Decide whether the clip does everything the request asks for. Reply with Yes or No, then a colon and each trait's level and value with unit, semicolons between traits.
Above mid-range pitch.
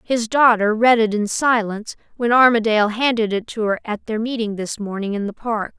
Yes: high, 220 Hz